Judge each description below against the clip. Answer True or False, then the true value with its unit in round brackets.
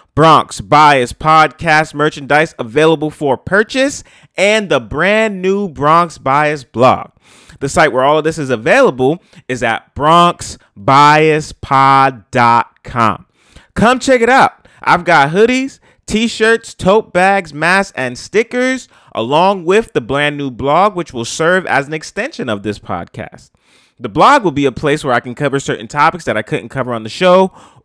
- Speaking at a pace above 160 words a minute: False (155 wpm)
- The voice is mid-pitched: True (150 Hz)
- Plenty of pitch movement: True (6.0 semitones)